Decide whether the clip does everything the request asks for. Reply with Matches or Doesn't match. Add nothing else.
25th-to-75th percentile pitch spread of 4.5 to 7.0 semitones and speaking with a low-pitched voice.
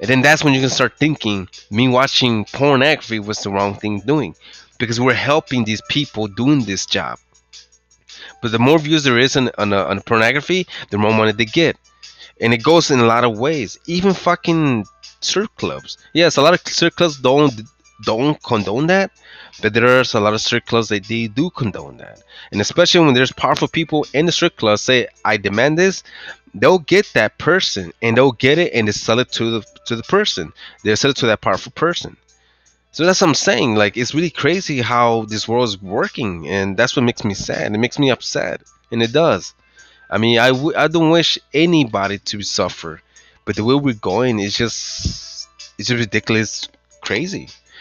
Matches